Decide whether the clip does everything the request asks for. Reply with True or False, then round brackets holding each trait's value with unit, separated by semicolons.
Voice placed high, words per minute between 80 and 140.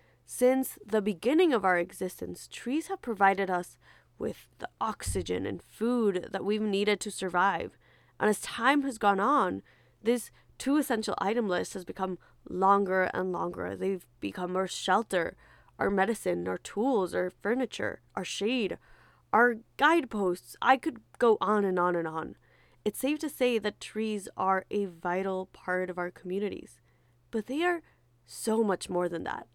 False (195 Hz; 160 wpm)